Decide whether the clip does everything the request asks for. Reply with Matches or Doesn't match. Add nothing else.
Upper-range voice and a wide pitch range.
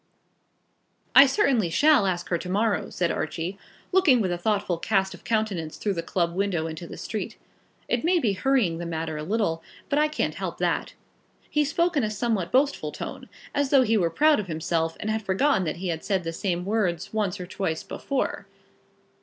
Matches